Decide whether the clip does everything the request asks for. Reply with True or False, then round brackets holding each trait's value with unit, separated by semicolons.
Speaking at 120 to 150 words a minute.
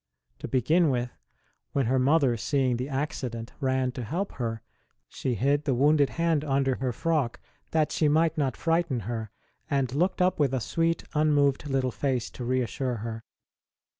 False (165 wpm)